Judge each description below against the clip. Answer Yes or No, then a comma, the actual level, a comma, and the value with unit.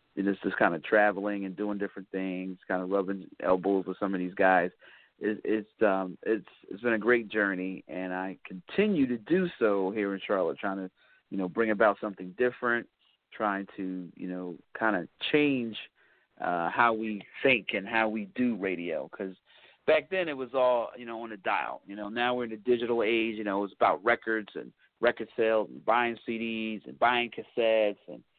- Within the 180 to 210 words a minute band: Yes, average, 200 wpm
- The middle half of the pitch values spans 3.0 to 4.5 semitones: Yes, average, 3.6 semitones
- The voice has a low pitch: Yes, low, 105 Hz